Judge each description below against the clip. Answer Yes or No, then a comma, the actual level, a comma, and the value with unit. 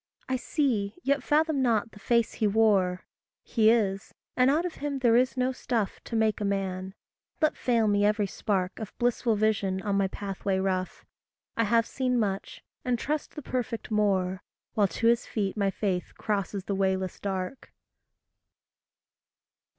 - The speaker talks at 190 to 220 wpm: No, average, 165 wpm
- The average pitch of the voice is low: No, high, 215 Hz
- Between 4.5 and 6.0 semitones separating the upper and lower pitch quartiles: No, average, 3.9 semitones